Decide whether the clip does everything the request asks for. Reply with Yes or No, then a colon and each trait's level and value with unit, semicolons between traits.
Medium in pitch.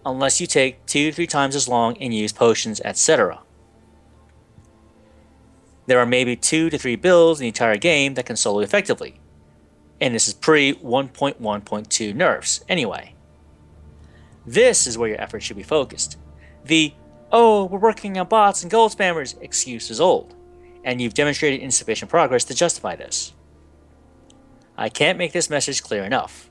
No: low, 120 Hz